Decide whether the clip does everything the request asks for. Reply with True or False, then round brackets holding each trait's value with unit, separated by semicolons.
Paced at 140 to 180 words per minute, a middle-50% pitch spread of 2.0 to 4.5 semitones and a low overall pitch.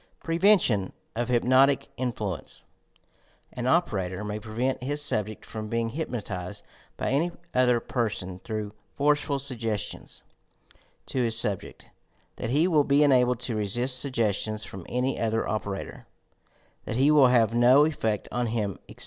True (150 wpm; 3.9 semitones; 120 Hz)